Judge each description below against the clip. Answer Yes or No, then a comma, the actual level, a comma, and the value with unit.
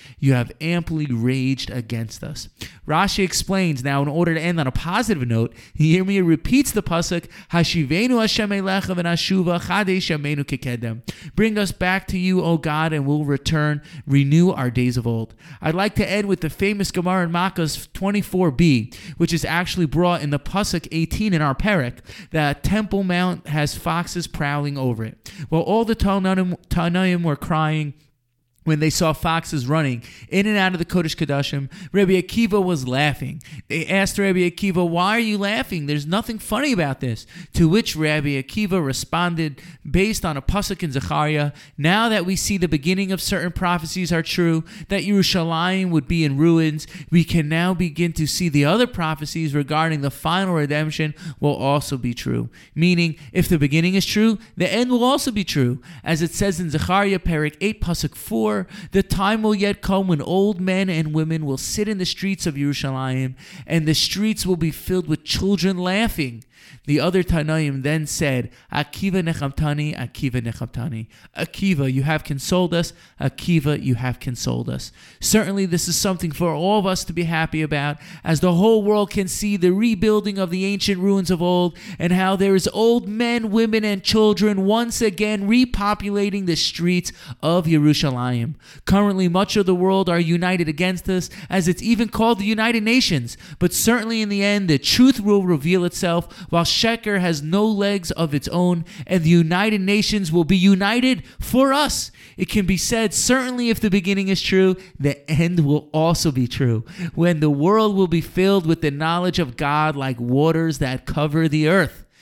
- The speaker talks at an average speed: Yes, average, 175 wpm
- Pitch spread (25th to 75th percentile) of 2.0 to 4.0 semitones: No, average, 4.5 semitones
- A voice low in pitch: No, medium, 170 Hz